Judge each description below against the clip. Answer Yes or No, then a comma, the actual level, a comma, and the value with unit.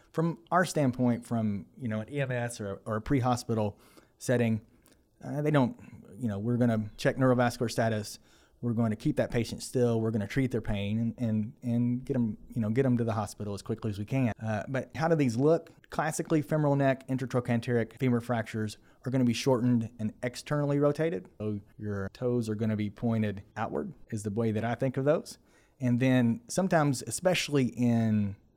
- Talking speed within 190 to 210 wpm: Yes, fast, 205 wpm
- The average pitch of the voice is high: No, low, 120 Hz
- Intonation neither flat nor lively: Yes, average, 3.4 semitones